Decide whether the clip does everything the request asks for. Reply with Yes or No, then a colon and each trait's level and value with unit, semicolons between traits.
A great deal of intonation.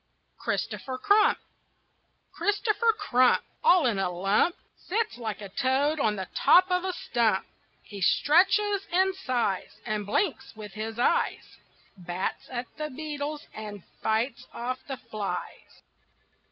Yes: wide, 9.0 semitones